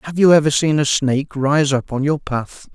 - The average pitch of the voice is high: No, medium, 145 Hz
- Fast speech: Yes, fast, 240 wpm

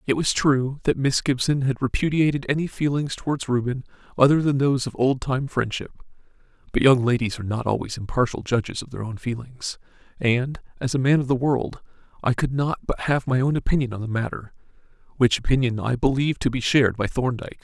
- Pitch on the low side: Yes, low, 130 Hz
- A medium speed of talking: Yes, average, 195 wpm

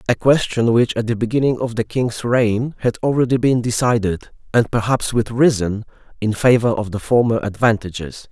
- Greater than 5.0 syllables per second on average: Yes, 5.2 syllables/s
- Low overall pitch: Yes, low, 115 Hz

